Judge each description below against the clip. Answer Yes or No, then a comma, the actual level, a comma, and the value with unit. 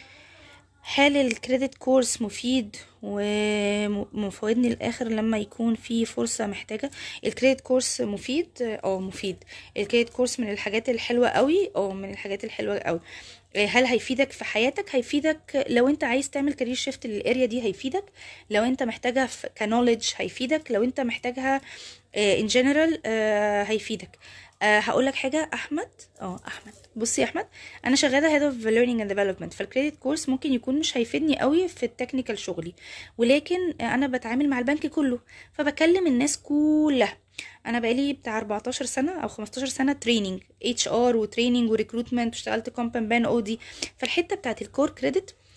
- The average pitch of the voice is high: Yes, high, 245 Hz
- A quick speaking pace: Yes, fast, 145 wpm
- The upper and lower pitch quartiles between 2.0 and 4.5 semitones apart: Yes, average, 3.9 semitones